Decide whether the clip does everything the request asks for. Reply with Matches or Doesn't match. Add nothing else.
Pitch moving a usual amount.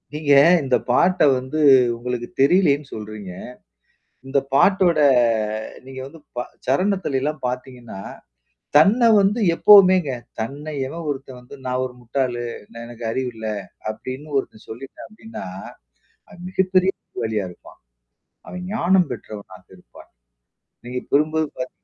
Doesn't match